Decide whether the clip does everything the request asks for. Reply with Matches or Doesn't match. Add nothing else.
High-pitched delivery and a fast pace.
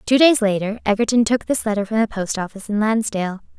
Matches